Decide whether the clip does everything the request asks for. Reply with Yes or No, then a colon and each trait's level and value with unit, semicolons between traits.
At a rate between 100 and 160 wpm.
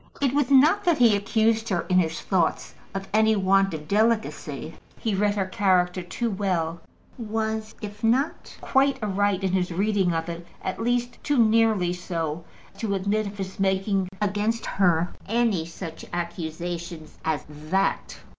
Yes: average, 155 wpm